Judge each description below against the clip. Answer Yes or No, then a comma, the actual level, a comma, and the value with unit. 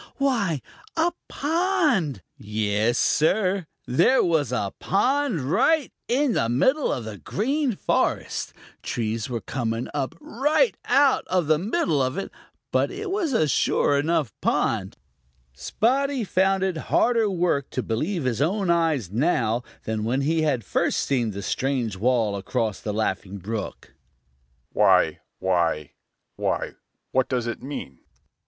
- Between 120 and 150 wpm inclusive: Yes, average, 140 wpm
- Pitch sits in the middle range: Yes, medium, 150 Hz